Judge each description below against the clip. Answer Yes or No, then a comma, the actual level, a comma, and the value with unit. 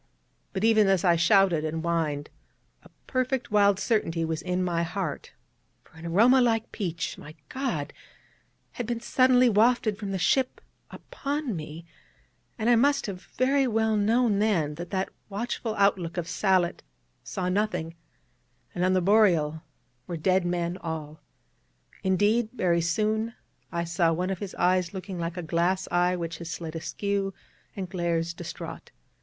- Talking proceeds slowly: No, average, 155 wpm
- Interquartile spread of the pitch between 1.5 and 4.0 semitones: No, average, 4.4 semitones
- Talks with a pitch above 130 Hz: Yes, medium, 185 Hz